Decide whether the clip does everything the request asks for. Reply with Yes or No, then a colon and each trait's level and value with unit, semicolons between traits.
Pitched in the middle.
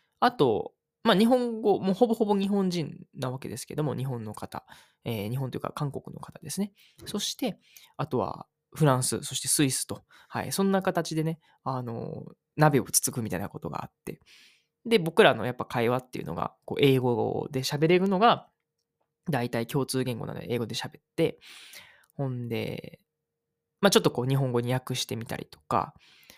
Yes: medium, 150 Hz